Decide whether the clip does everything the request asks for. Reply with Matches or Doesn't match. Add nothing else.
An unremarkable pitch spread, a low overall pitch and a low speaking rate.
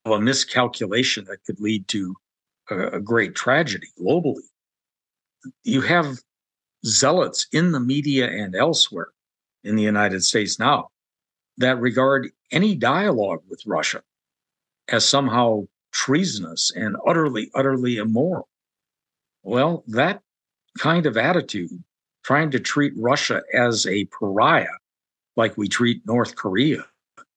Matches